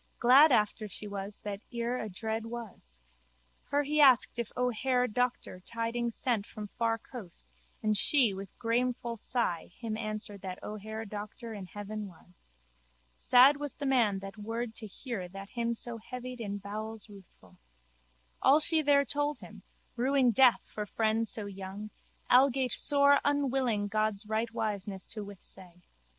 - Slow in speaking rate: No, average, 150 wpm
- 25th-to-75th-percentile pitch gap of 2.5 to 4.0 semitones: Yes, average, 3.4 semitones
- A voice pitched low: No, high, 225 Hz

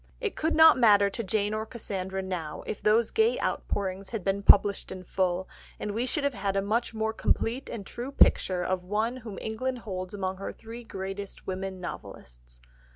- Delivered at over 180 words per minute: Yes, average, 190 wpm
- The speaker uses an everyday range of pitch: Yes, average, 3.4 semitones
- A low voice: No, high, 200 Hz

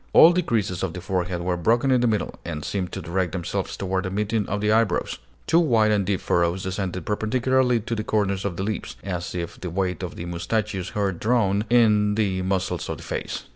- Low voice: Yes, low, 100 Hz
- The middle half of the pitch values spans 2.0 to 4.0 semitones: Yes, average, 3.1 semitones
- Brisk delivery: Yes, fast, 220 wpm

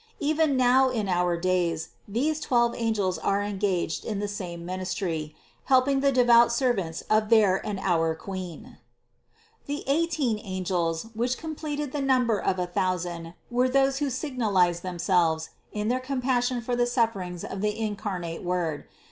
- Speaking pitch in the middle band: No, high, 210 Hz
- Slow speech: No, average, 155 wpm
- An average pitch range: No, wide, 6.1 semitones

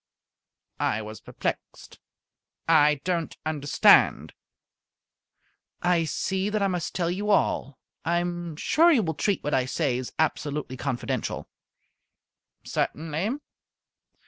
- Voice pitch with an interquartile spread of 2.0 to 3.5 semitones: No, average, 4.0 semitones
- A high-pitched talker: No, medium, 165 Hz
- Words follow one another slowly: Yes, slow, 115 wpm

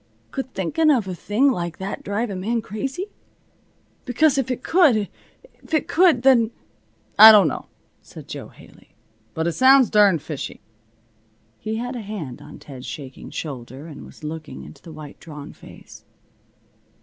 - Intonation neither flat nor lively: No, wide, 8.2 semitones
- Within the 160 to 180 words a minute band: Yes, average, 165 wpm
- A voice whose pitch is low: No, high, 210 Hz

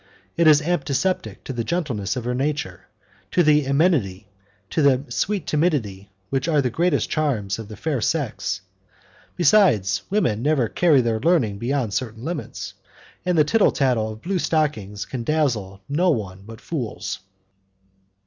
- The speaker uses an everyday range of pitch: No, wide, 6.4 semitones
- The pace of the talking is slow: No, average, 155 wpm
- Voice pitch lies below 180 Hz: Yes, low, 135 Hz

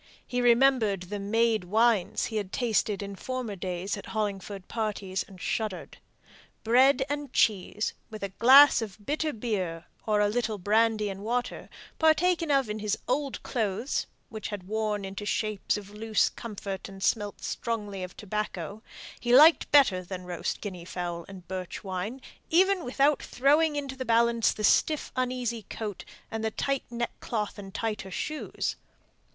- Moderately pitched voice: No, high, 215 Hz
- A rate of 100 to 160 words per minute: Yes, average, 155 wpm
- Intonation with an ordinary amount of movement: Yes, average, 3.9 semitones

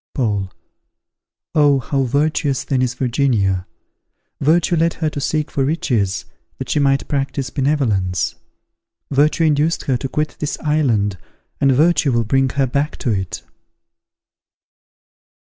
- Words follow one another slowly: Yes, slow, 130 wpm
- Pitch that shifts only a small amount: No, average, 3.9 semitones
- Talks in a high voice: No, low, 135 Hz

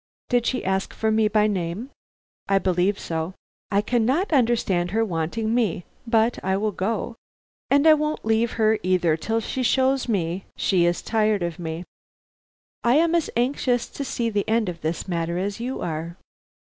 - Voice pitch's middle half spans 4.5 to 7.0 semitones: Yes, average, 5.1 semitones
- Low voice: No, high, 215 Hz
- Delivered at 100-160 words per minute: No, average, 175 wpm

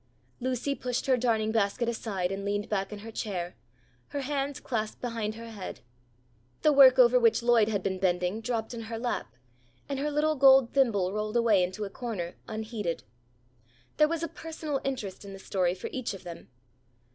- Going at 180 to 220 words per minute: Yes, average, 185 wpm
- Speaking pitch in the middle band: No, high, 225 Hz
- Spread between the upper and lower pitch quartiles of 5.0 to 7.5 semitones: No, average, 4.5 semitones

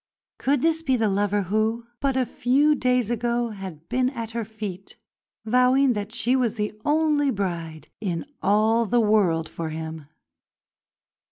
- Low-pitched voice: No, high, 225 Hz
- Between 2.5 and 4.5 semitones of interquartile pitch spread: Yes, average, 4.1 semitones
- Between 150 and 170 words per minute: Yes, average, 155 wpm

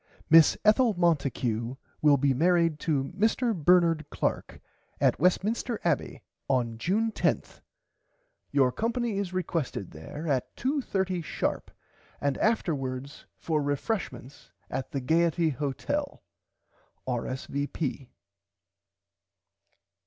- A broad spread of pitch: Yes, wide, 6.0 semitones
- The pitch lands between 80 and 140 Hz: No, medium, 160 Hz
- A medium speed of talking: No, slow, 100 wpm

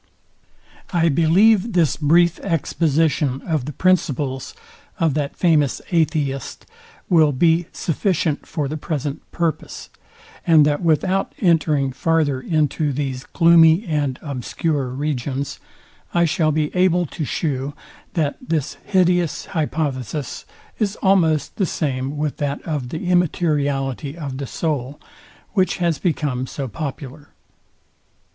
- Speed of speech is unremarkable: No, slow, 120 wpm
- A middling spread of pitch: Yes, average, 3.2 semitones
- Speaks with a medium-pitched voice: Yes, medium, 155 Hz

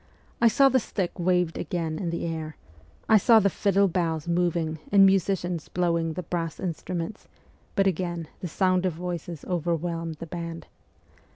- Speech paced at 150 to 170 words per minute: Yes, average, 160 wpm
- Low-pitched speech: No, medium, 175 Hz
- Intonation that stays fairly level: Yes, narrow, 2.1 semitones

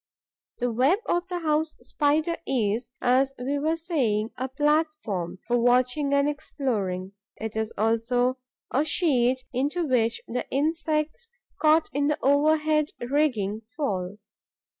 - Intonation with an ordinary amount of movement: Yes, average, 4.4 semitones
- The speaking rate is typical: No, slow, 130 wpm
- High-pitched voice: Yes, very high, 270 Hz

